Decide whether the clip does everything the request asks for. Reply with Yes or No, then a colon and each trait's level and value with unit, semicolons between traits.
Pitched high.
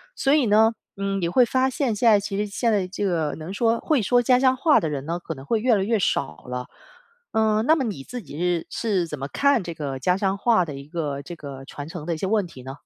Yes: high, 195 Hz